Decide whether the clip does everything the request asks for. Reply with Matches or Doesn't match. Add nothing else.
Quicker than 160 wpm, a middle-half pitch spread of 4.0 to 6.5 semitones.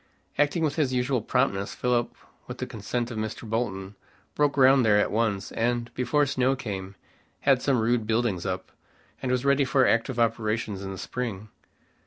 Doesn't match